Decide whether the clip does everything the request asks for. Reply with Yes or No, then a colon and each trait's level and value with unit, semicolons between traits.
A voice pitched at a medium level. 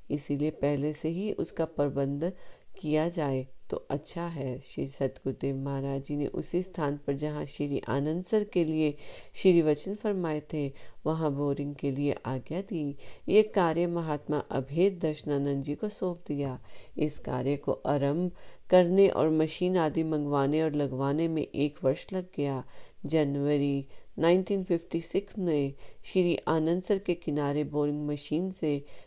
Yes: medium, 150 Hz